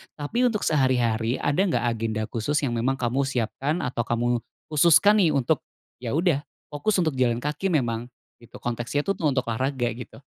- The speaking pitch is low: Yes, low, 130 Hz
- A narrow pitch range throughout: No, average, 4.1 semitones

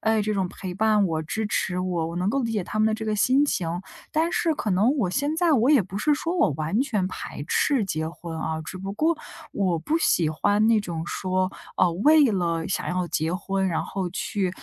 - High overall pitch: Yes, high, 195 Hz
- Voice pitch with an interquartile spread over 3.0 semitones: Yes, average, 4.5 semitones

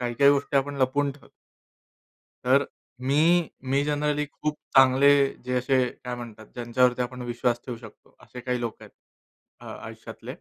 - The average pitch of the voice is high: No, low, 130 Hz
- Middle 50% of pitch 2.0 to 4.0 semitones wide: Yes, narrow, 2.4 semitones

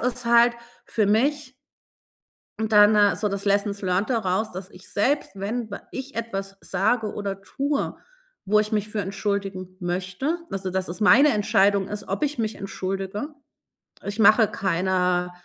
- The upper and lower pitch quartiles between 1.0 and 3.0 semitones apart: Yes, average, 2.7 semitones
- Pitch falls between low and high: No, high, 205 Hz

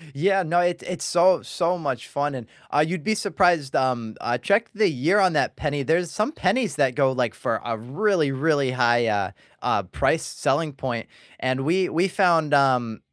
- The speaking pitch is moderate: Yes, medium, 150 Hz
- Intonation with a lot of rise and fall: Yes, wide, 5.7 semitones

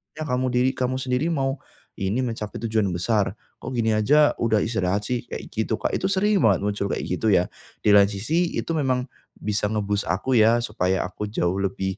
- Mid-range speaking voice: No, low, 110 Hz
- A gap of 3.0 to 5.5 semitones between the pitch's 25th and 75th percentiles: Yes, average, 4.3 semitones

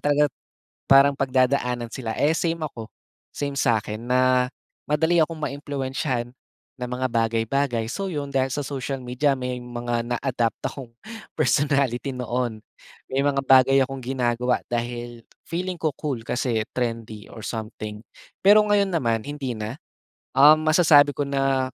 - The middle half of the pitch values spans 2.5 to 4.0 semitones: Yes, average, 3.1 semitones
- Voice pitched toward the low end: Yes, low, 130 Hz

